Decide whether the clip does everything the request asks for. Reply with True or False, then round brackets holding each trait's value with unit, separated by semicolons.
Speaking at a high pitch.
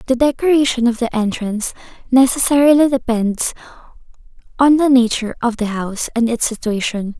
True (245 Hz)